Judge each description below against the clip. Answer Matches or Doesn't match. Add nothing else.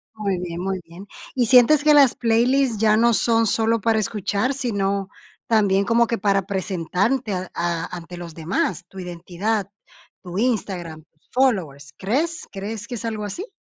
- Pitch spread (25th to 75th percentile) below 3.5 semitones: Doesn't match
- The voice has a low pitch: Doesn't match